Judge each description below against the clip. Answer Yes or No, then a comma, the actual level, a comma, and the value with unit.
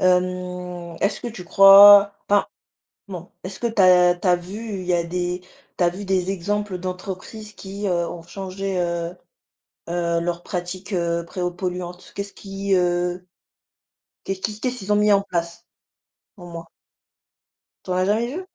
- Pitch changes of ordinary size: No, narrow, 2.1 semitones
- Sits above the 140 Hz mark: Yes, medium, 185 Hz